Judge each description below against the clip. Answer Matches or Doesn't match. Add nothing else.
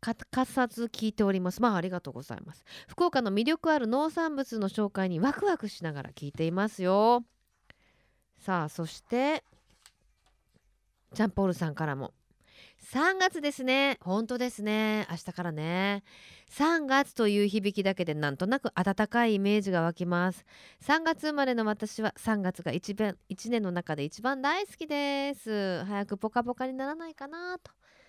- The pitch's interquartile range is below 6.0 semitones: Doesn't match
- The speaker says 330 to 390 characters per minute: Doesn't match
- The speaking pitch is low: Doesn't match